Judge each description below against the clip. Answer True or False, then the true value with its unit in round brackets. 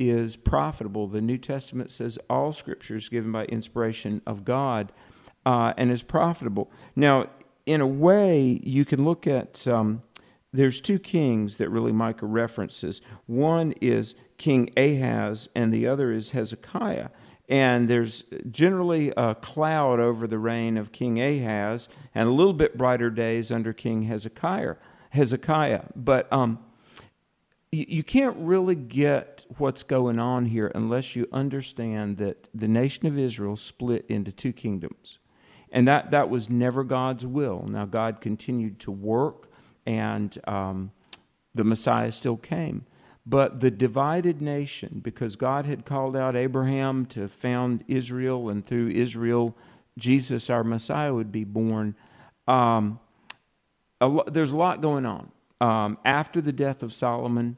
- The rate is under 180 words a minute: True (145 wpm)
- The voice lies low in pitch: True (120 Hz)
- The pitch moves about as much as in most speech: True (3.3 semitones)